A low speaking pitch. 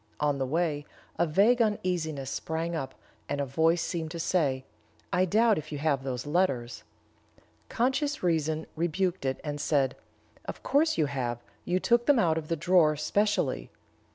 No: medium, 160 Hz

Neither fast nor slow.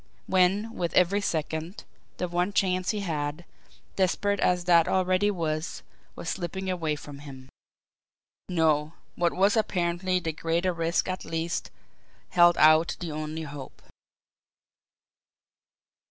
No: slow, 125 wpm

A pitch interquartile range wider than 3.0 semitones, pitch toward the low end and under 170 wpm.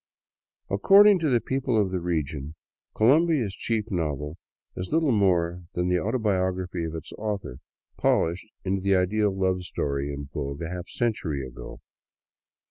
Yes: average, 4.9 semitones; very low, 95 Hz; average, 145 wpm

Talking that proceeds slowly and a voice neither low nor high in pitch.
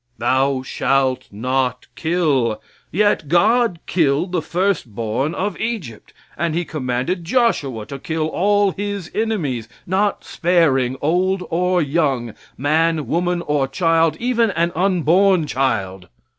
Yes: slow, 125 wpm; medium, 165 Hz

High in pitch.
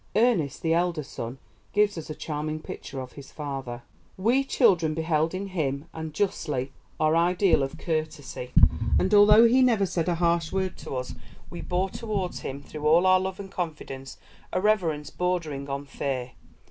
No: medium, 165 Hz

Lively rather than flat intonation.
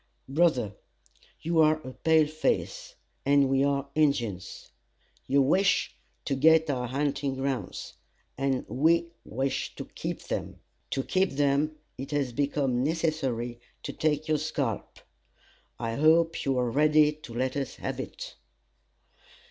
No: average, 2.9 semitones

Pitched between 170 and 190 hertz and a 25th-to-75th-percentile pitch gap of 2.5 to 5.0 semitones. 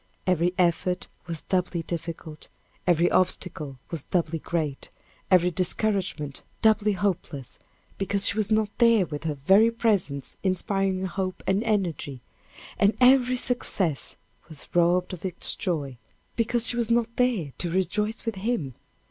Yes: medium, 185 Hz; average, 4.5 semitones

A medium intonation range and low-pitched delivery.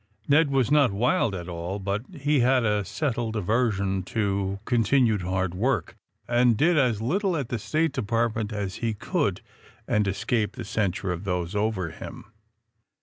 Yes: average, 4.4 semitones; low, 110 Hz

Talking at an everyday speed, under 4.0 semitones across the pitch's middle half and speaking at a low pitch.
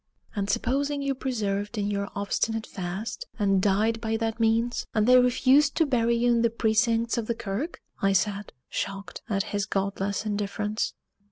No: average, 170 wpm; average, 2.9 semitones; high, 220 Hz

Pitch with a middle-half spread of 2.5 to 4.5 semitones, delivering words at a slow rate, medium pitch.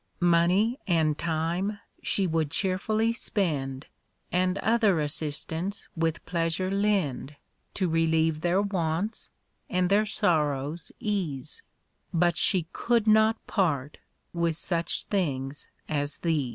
Yes: average, 4.1 semitones; slow, 110 wpm; medium, 170 Hz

